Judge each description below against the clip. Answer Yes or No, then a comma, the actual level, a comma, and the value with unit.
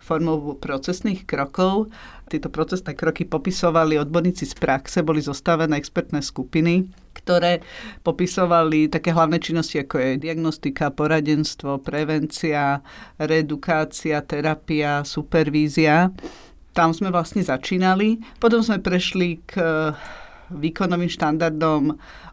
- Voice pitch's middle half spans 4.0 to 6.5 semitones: No, average, 2.7 semitones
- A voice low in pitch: No, medium, 160 Hz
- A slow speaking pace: Yes, slow, 100 wpm